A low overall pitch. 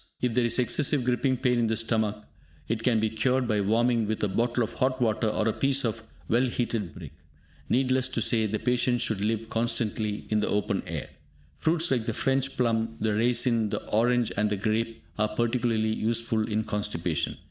Yes: low, 115 Hz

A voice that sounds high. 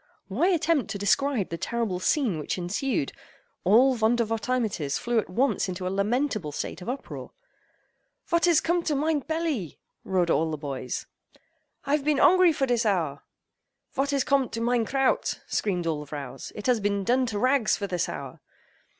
Yes: high, 230 Hz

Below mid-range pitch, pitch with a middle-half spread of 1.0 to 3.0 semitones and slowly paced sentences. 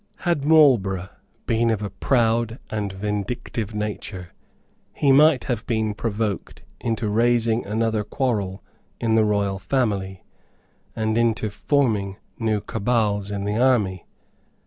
Yes: low, 110 Hz; narrow, 2.5 semitones; slow, 125 wpm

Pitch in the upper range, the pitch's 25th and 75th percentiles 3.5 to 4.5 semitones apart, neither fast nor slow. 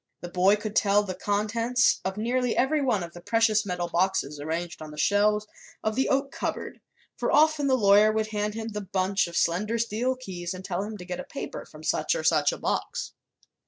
No: high, 210 Hz; average, 3.9 semitones; fast, 215 wpm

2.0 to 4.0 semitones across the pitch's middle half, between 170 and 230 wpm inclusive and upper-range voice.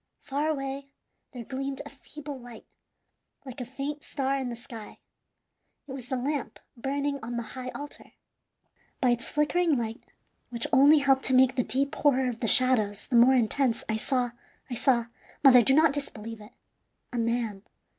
Yes: average, 2.7 semitones; average, 175 wpm; very high, 260 Hz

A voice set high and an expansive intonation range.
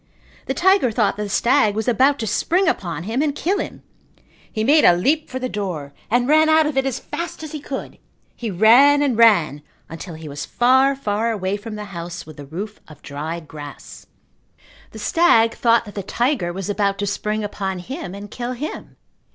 Yes: high, 220 Hz; wide, 6.3 semitones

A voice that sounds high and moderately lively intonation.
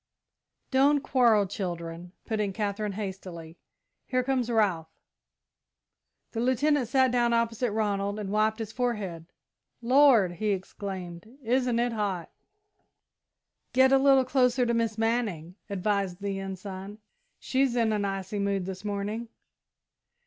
Yes: high, 215 Hz; average, 4.0 semitones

